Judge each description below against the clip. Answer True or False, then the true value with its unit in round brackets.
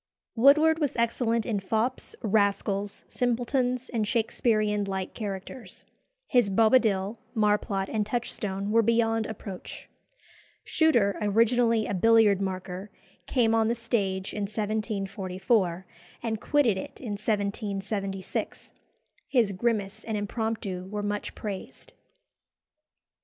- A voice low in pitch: False (215 Hz)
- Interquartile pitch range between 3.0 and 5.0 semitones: False (2.6 semitones)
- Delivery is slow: True (110 wpm)